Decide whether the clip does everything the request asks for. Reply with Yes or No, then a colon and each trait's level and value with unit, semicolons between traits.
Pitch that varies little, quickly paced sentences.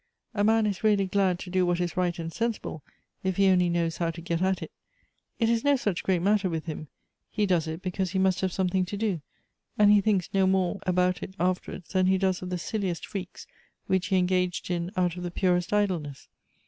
Yes: narrow, 1.9 semitones; fast, 225 wpm